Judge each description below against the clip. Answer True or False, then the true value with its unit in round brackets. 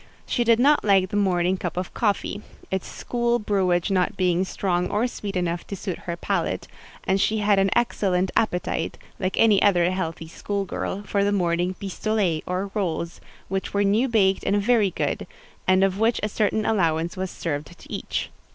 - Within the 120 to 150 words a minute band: False (185 wpm)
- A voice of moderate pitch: False (195 Hz)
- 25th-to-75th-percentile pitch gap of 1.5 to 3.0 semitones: True (2.6 semitones)